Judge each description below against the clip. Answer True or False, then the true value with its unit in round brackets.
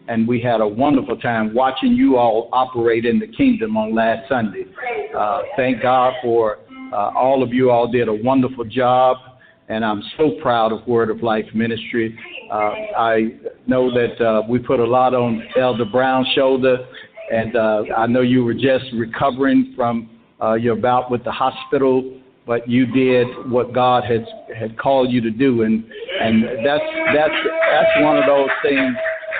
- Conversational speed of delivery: True (175 wpm)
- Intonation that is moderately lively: False (2.3 semitones)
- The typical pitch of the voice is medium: False (125 Hz)